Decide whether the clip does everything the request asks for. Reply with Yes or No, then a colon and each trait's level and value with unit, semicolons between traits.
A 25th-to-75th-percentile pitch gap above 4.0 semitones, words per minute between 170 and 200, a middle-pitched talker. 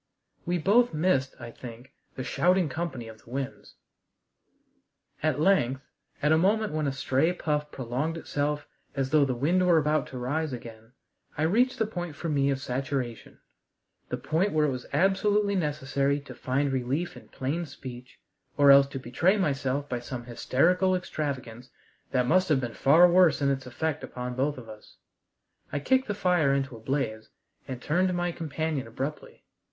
Yes: average, 4.9 semitones; average, 175 wpm; medium, 145 Hz